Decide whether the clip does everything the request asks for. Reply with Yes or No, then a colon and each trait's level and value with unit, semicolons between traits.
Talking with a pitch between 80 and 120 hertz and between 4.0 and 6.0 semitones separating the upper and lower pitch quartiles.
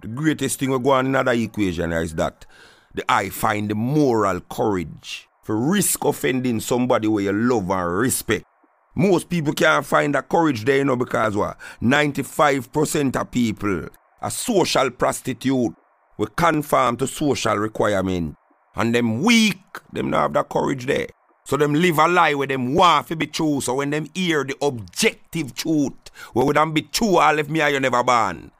No: low, 135 Hz; average, 5.0 semitones